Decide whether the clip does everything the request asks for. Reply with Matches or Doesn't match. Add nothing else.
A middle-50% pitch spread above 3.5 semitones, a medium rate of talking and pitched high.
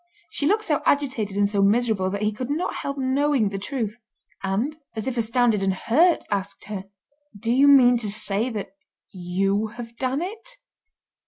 Matches